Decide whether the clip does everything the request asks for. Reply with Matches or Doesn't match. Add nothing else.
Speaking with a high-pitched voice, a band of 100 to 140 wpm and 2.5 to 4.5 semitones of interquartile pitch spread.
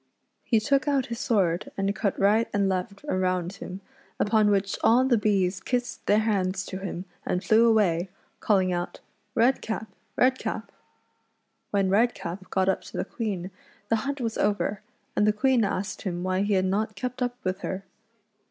Doesn't match